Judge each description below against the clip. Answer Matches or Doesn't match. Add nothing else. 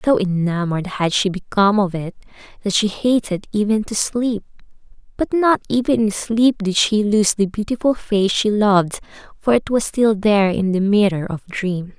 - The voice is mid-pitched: Doesn't match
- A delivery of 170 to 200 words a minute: Matches